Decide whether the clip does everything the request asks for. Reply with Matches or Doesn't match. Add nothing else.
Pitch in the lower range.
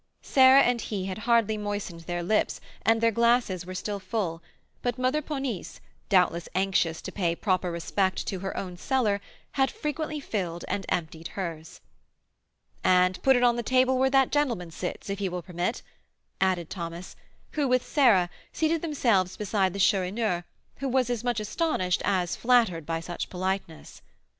Doesn't match